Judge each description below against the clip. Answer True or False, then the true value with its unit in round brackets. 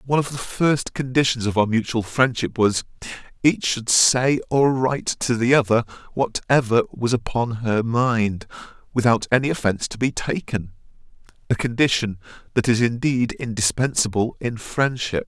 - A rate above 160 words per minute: False (145 wpm)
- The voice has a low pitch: True (120 Hz)